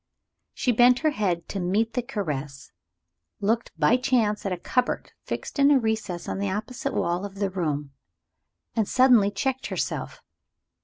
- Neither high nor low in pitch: No, high, 210 Hz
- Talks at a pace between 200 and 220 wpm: No, average, 160 wpm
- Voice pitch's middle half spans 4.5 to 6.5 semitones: Yes, average, 5.0 semitones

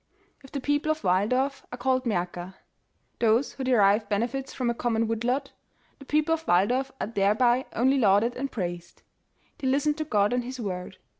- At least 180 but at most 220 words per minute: Yes, average, 190 wpm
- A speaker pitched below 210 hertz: No, high, 245 Hz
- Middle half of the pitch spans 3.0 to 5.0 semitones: Yes, average, 4.7 semitones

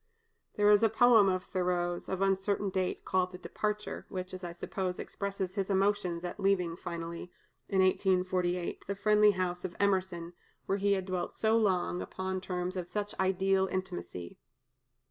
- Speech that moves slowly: No, average, 165 wpm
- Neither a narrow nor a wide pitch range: No, narrow, 1.7 semitones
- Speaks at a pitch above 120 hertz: Yes, medium, 185 Hz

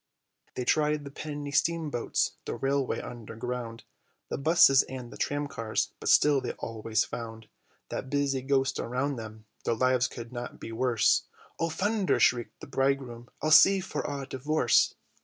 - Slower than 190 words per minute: Yes, average, 160 wpm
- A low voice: Yes, low, 130 Hz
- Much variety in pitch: No, average, 3.5 semitones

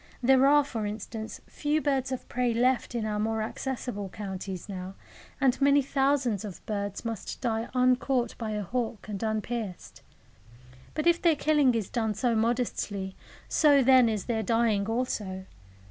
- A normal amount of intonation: Yes, average, 3.7 semitones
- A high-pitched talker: Yes, high, 230 Hz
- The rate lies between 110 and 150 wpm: No, average, 160 wpm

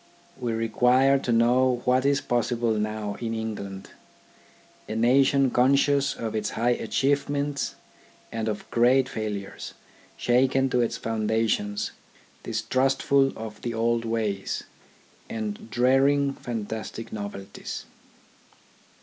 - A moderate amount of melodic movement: Yes, average, 3.1 semitones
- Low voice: Yes, low, 115 Hz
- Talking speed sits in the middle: No, slow, 115 wpm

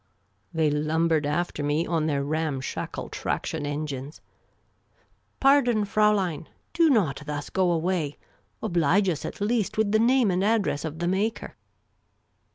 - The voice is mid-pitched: Yes, medium, 170 Hz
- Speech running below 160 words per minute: Yes, average, 140 wpm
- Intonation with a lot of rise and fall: Yes, wide, 5.7 semitones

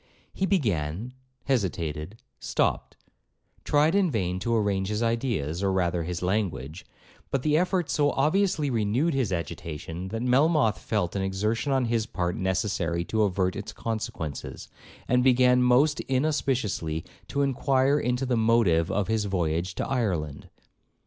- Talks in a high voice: No, low, 110 Hz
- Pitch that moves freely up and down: Yes, wide, 6.4 semitones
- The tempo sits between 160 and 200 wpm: No, slow, 135 wpm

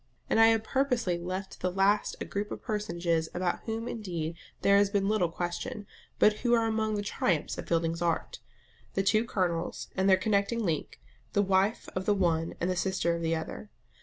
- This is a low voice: No, high, 195 Hz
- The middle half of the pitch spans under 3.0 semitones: No, average, 3.8 semitones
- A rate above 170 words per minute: Yes, average, 200 wpm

